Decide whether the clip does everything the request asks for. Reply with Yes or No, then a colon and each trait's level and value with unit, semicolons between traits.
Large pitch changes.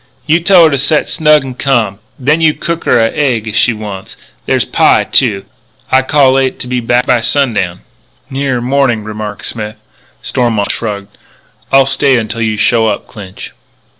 No: average, 4.2 semitones